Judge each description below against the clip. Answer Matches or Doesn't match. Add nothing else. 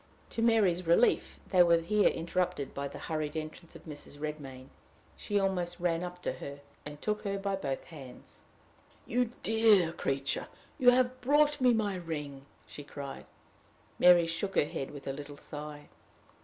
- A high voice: Doesn't match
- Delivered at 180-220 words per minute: Doesn't match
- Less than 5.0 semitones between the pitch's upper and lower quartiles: Doesn't match